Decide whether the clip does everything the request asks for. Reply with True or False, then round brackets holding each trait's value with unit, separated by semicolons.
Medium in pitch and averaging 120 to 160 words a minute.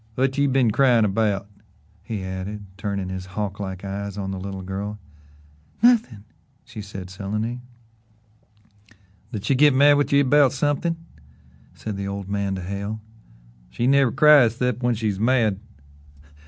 False (105 Hz; 150 wpm)